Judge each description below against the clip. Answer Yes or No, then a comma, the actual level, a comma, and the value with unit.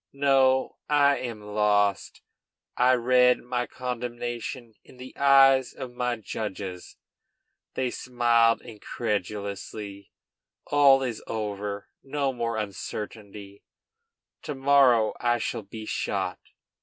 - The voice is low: Yes, low, 120 Hz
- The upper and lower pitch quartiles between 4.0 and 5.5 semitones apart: No, average, 3.5 semitones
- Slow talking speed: Yes, slow, 105 wpm